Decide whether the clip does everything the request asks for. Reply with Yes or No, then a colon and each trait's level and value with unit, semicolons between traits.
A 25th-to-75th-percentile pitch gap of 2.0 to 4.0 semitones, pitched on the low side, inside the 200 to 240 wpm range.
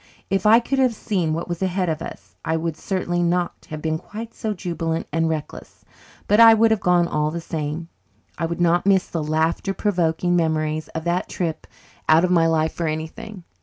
No: average, 3.0 semitones; medium, 170 Hz; fast, 205 wpm